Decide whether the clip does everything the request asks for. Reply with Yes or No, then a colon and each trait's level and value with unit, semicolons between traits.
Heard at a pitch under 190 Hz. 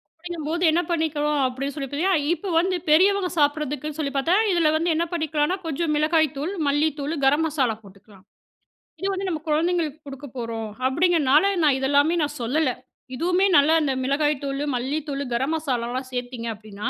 No: very high, 295 Hz